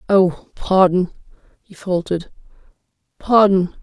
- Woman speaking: Yes, female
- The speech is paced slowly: Yes, slow, 80 wpm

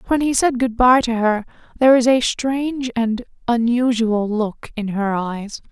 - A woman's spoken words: Yes, female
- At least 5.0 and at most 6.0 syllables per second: No, 4.3 syllables/s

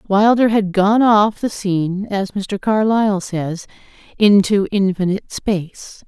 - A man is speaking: No, female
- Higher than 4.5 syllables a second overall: No, 4.0 syllables/s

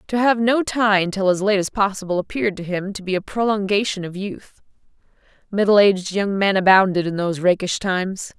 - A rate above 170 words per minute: Yes, average, 195 wpm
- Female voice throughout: Yes, female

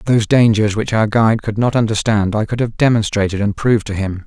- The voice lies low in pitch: Yes, low, 110 Hz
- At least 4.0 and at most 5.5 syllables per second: No, 6.1 syllables/s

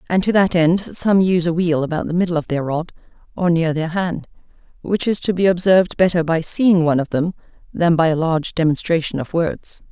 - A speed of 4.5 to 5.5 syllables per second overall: No, 5.7 syllables/s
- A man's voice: No, female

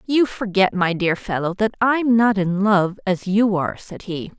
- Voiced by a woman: Yes, female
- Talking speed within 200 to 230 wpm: Yes, fast, 205 wpm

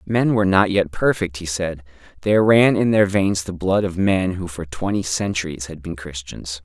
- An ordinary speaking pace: No, fast, 210 wpm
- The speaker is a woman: No, male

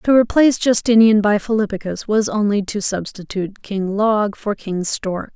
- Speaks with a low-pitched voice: No, high, 210 Hz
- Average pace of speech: Yes, average, 155 wpm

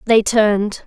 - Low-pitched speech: No, high, 220 Hz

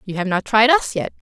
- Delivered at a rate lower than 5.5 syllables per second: No, 5.7 syllables/s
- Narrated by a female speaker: Yes, female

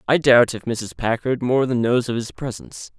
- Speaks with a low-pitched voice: Yes, low, 120 Hz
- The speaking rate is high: Yes, fast, 220 wpm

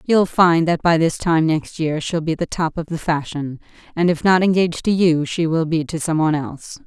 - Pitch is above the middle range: No, medium, 165 Hz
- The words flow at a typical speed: No, fast, 245 wpm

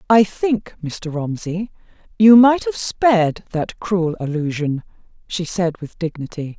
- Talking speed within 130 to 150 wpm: Yes, slow, 135 wpm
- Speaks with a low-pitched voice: No, medium, 185 Hz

